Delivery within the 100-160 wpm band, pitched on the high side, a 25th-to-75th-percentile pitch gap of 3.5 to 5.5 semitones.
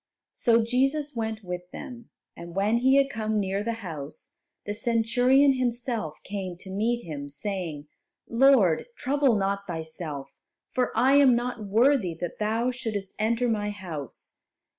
Yes: average, 145 wpm; high, 220 Hz; average, 5.0 semitones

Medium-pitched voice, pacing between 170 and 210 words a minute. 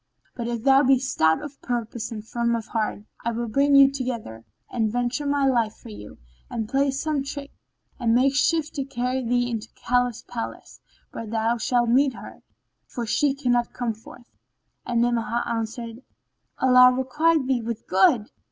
No: high, 245 Hz; average, 175 wpm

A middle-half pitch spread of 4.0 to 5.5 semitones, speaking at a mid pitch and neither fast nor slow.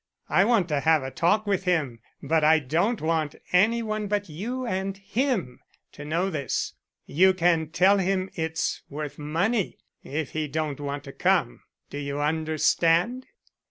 Yes: average, 4.7 semitones; medium, 165 Hz; average, 160 wpm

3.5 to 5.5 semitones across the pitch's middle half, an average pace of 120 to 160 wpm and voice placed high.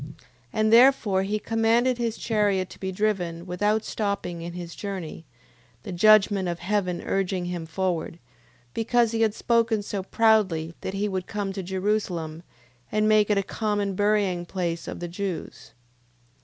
No: average, 3.1 semitones; average, 155 wpm; high, 200 Hz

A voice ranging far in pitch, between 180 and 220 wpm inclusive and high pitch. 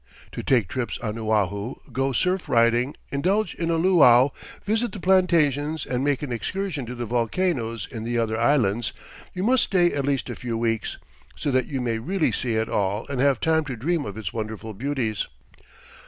No: wide, 5.9 semitones; average, 190 wpm; low, 130 Hz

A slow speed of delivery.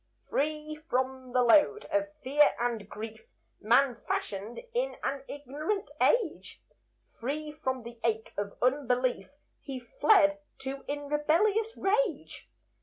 Yes: slow, 120 wpm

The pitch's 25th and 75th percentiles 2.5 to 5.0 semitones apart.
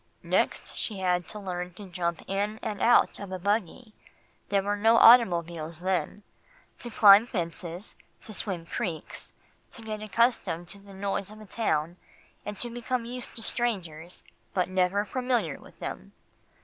Yes: average, 3.8 semitones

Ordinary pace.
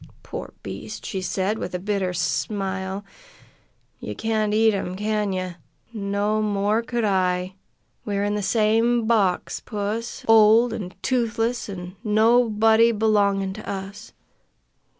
No: slow, 130 wpm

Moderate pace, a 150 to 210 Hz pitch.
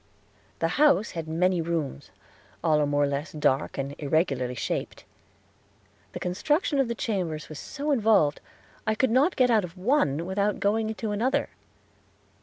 Yes: average, 155 wpm; medium, 185 Hz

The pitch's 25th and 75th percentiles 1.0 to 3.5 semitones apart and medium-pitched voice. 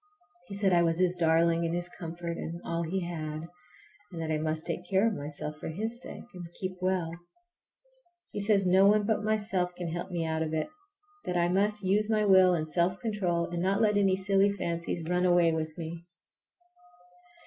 Yes: average, 2.8 semitones; medium, 175 Hz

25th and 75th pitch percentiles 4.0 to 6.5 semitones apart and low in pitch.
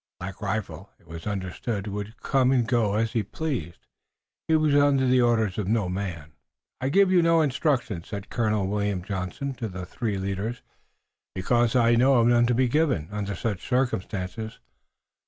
Yes: average, 4.7 semitones; low, 110 Hz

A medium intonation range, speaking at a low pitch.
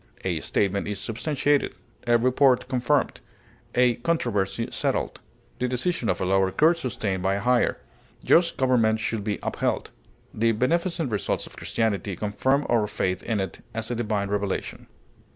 Yes: average, 4.1 semitones; low, 115 Hz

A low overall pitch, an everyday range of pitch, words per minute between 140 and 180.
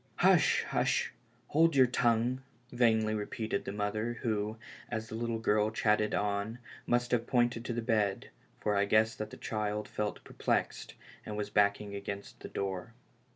No: low, 110 Hz; narrow, 2.1 semitones; average, 165 wpm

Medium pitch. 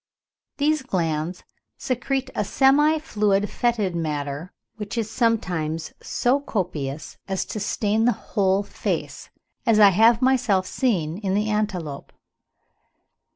No: high, 210 Hz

